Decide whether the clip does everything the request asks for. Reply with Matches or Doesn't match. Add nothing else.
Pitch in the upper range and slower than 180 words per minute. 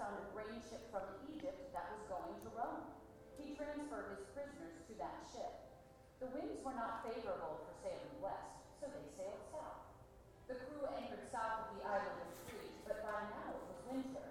Doesn't match